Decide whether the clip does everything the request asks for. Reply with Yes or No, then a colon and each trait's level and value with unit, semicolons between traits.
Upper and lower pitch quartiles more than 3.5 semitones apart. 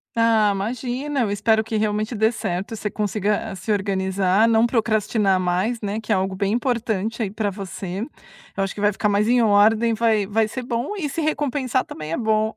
No: narrow, 2.6 semitones